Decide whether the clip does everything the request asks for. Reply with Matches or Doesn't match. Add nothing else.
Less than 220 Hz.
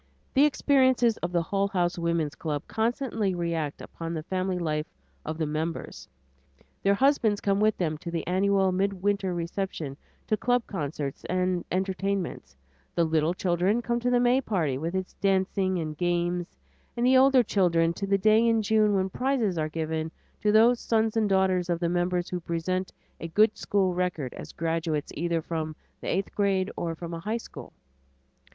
Matches